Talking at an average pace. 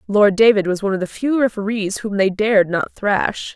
No: fast, 220 wpm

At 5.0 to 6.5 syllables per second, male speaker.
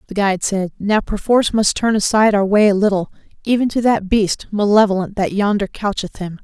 No: 5.7 syllables/s; female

